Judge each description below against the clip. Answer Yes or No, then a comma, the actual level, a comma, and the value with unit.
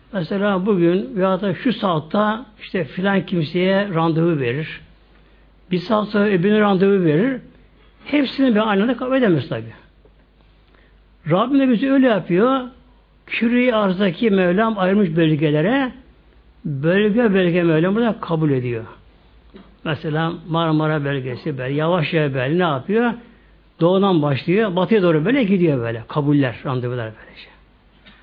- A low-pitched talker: No, medium, 180 Hz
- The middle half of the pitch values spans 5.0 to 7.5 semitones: Yes, wide, 5.6 semitones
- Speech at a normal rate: Yes, average, 125 wpm